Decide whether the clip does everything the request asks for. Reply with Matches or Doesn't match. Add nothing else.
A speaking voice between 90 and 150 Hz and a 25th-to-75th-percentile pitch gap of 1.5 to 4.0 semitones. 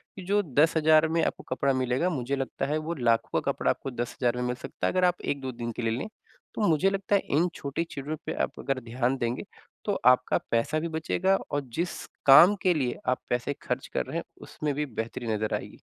Doesn't match